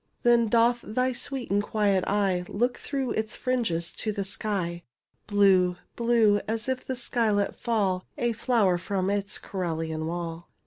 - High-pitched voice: Yes, high, 205 Hz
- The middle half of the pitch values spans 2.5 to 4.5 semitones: Yes, average, 4.2 semitones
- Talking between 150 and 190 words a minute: Yes, average, 155 wpm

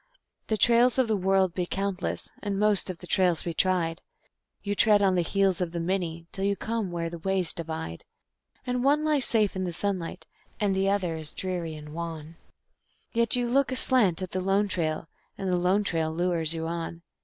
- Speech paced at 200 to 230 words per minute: Yes, fast, 205 wpm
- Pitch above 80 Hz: Yes, medium, 185 Hz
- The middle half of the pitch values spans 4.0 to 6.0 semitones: No, average, 3.4 semitones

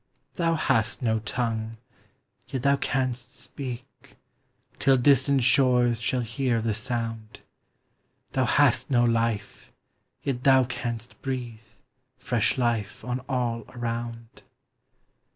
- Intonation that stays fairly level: Yes, narrow, 2.1 semitones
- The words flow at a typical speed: No, slow, 110 wpm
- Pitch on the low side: Yes, low, 120 Hz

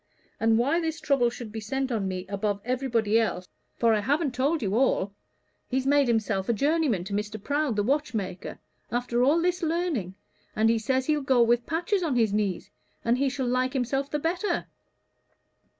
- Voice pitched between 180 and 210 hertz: No, high, 245 Hz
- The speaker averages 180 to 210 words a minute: Yes, average, 185 wpm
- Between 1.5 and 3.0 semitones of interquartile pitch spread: No, average, 4.7 semitones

